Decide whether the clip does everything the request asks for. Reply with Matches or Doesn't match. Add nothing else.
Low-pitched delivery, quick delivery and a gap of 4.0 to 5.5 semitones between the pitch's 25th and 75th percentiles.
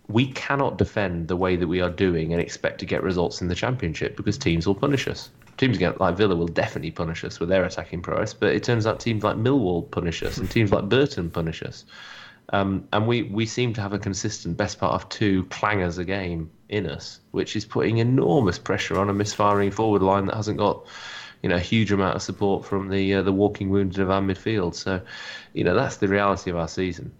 Doesn't match